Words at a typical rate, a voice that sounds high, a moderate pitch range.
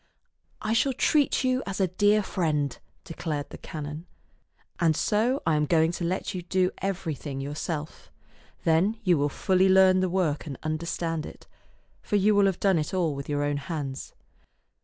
No: average, 180 wpm; medium, 170 Hz; average, 4.2 semitones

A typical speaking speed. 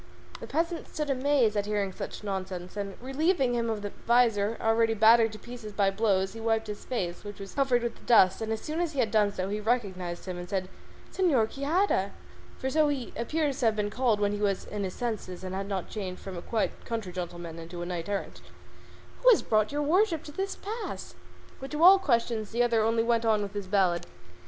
No: fast, 225 wpm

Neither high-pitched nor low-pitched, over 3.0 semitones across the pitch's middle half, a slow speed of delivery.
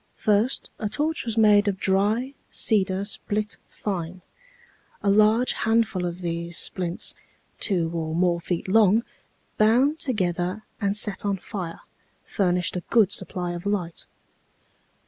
No: high, 200 Hz; average, 3.4 semitones; slow, 130 wpm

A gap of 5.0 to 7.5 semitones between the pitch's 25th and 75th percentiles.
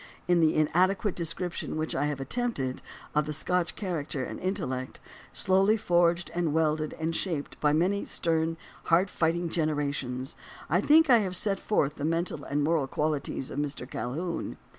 No: average, 3.5 semitones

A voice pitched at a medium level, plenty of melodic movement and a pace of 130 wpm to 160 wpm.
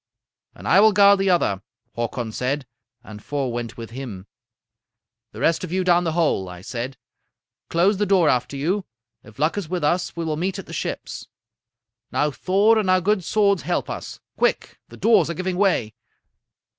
No: medium, 170 Hz; wide, 7.3 semitones; average, 185 wpm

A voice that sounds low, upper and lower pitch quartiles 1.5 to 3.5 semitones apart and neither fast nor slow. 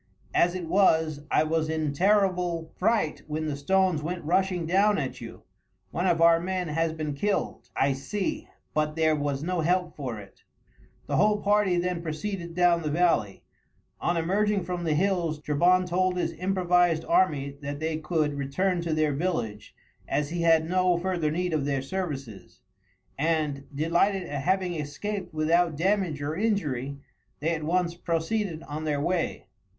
No: medium, 165 Hz; average, 3.2 semitones; average, 165 wpm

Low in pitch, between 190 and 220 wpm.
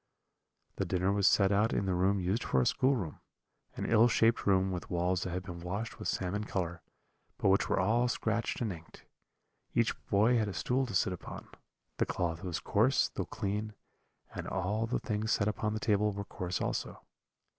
Yes: low, 100 Hz; average, 195 wpm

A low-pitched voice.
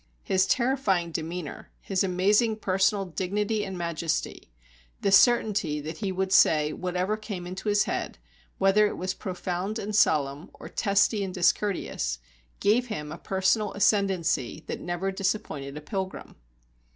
No: high, 190 Hz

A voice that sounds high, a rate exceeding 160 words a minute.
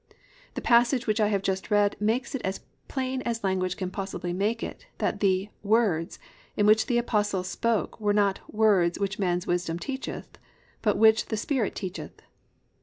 Yes: high, 210 Hz; average, 175 wpm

